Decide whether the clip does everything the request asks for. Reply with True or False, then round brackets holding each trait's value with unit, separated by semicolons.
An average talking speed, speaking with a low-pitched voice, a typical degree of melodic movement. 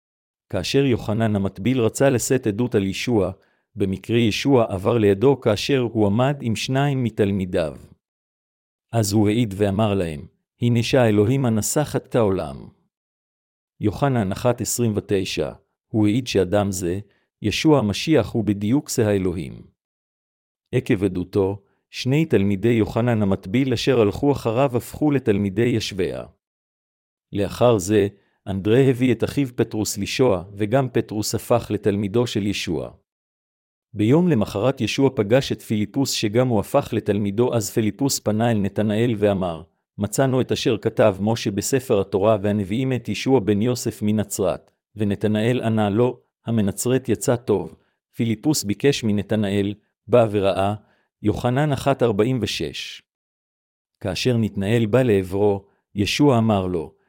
True (120 wpm; 110 Hz; 3.5 semitones)